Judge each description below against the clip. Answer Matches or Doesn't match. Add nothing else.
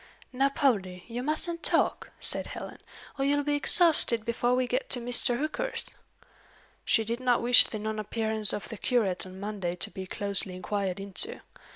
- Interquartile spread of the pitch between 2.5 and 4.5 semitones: Doesn't match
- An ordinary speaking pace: Matches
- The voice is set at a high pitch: Matches